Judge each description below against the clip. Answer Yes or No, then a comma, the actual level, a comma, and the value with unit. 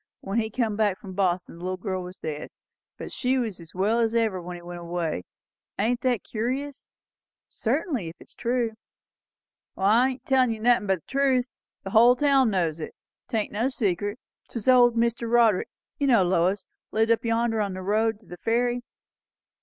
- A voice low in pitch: No, high, 220 Hz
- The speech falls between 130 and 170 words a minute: No, average, 185 wpm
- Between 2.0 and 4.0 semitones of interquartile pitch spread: No, average, 4.4 semitones